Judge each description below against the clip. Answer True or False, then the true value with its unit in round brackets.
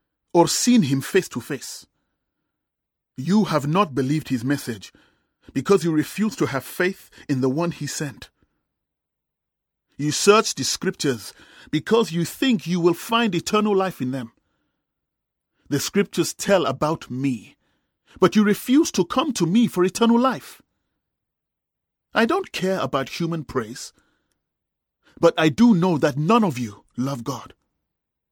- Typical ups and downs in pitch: False (6.7 semitones)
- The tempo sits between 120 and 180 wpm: True (145 wpm)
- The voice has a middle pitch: True (165 Hz)